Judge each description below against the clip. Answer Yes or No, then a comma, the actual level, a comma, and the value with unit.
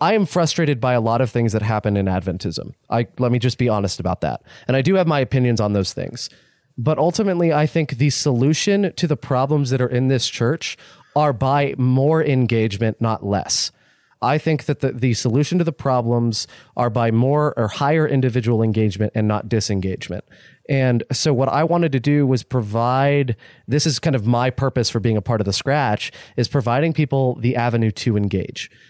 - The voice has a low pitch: Yes, low, 125 Hz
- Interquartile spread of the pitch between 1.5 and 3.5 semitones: No, average, 4.3 semitones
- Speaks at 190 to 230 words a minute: Yes, average, 200 wpm